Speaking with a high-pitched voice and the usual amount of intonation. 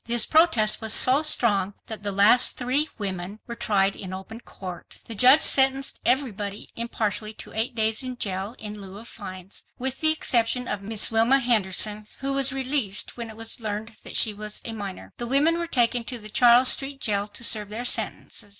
Yes: high, 225 Hz; average, 3.6 semitones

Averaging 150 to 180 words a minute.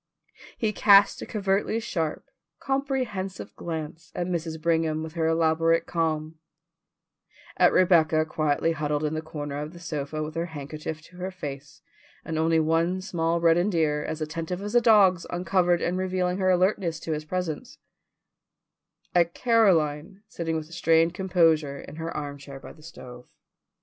Yes: average, 155 wpm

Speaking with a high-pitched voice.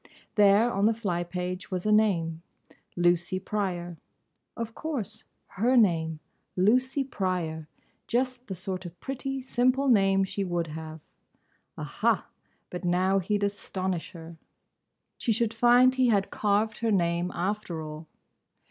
Yes: high, 195 Hz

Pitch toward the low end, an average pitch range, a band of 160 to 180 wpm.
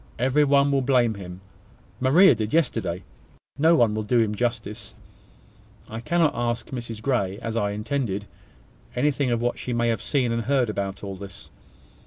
Yes: low, 120 Hz; average, 4.0 semitones; average, 170 wpm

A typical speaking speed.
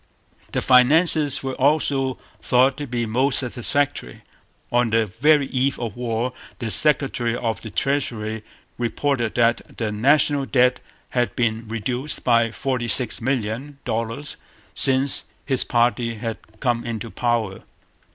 No: slow, 130 wpm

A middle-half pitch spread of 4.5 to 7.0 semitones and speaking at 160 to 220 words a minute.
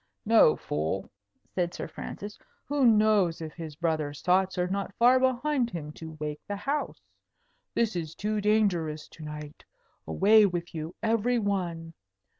No: average, 5.2 semitones; average, 145 wpm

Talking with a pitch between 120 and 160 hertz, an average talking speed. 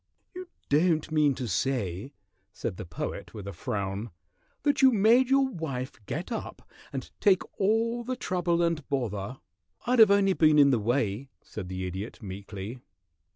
Yes: medium, 140 Hz; average, 165 wpm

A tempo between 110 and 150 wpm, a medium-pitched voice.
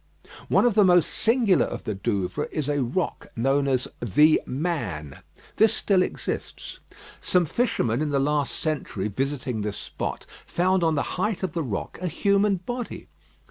No: average, 165 wpm; medium, 150 Hz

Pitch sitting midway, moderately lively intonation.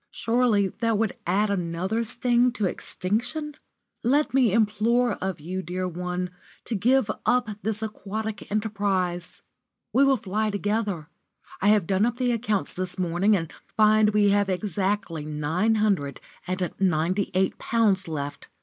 No: high, 205 Hz; average, 3.4 semitones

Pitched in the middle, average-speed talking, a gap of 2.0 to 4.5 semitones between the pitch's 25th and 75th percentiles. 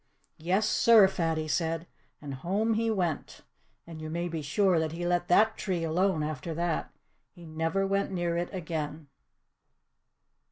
Yes: medium, 170 Hz; average, 155 wpm; average, 3.2 semitones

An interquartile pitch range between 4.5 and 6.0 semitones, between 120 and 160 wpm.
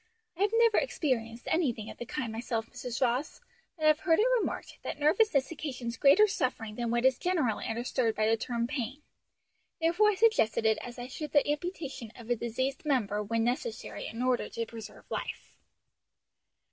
No: average, 5.0 semitones; average, 180 wpm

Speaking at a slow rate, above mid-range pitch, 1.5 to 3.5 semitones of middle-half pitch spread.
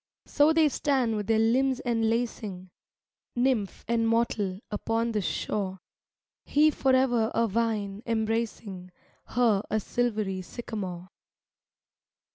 Yes: slow, 105 wpm; high, 225 Hz; average, 2.8 semitones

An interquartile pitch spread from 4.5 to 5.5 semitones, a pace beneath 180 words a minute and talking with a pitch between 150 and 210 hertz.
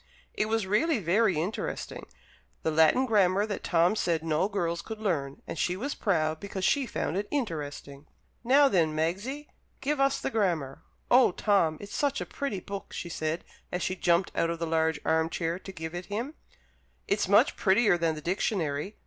No: average, 5.1 semitones; average, 190 wpm; medium, 185 Hz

